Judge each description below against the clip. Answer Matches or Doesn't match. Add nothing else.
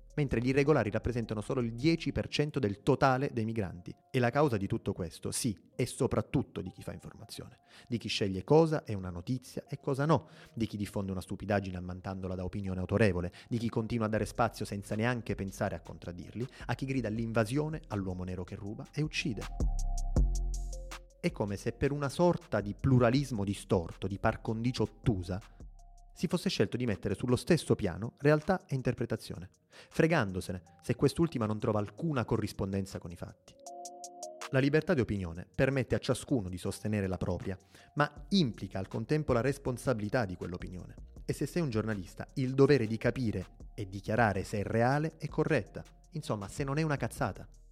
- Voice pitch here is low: Matches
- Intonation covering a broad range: Matches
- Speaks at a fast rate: Matches